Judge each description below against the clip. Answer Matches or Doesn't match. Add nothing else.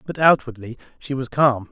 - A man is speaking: Matches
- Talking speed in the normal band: Matches